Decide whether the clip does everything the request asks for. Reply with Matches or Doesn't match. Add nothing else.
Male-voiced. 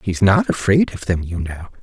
Matches